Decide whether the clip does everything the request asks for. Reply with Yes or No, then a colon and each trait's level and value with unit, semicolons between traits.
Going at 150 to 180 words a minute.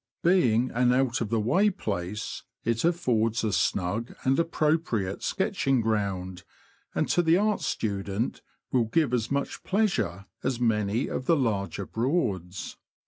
No: average, 140 wpm